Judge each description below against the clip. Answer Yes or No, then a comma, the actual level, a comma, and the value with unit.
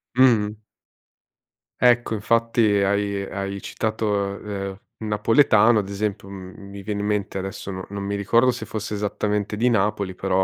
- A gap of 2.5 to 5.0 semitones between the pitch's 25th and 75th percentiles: No, narrow, 1.8 semitones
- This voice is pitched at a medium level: No, low, 105 Hz